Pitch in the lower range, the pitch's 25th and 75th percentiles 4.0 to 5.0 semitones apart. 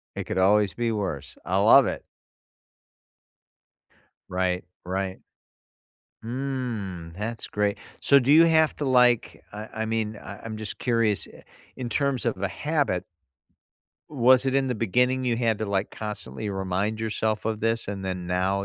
Yes: low, 110 Hz; average, 4.3 semitones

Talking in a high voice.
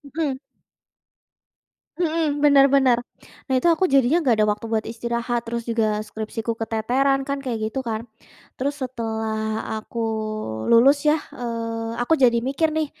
Yes: high, 240 Hz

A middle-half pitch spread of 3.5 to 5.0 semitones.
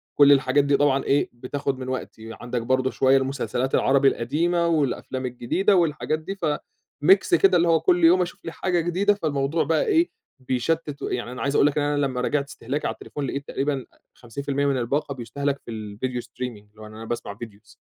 Yes: average, 3.8 semitones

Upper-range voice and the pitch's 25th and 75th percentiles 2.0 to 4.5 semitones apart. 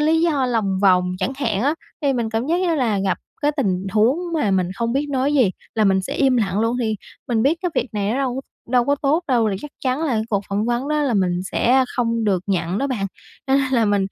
No: high, 235 Hz; average, 5.3 semitones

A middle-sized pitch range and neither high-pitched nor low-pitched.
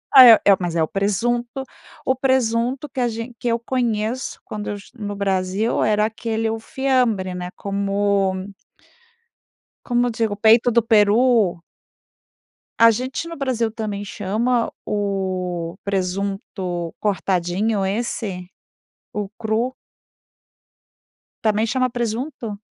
No: average, 3.3 semitones; high, 215 Hz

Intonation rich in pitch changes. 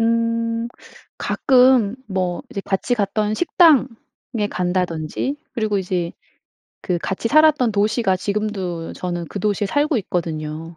No: average, 4.3 semitones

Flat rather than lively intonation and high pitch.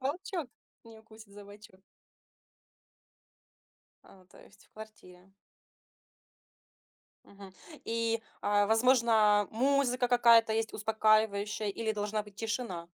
Yes: narrow, 2.0 semitones; high, 220 Hz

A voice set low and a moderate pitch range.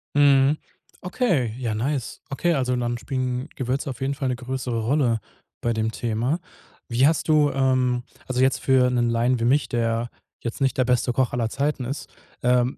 No: low, 125 Hz; narrow, 2.3 semitones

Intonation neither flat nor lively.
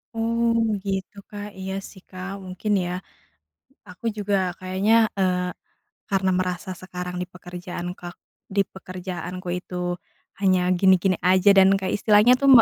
No: narrow, 1.9 semitones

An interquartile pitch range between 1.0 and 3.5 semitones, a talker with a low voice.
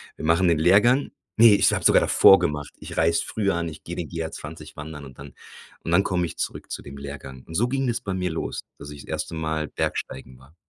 No: average, 4.0 semitones; very low, 80 Hz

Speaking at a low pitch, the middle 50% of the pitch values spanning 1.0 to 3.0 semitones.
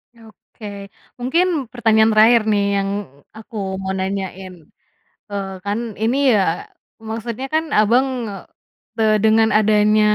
No: high, 215 Hz; narrow, 2.4 semitones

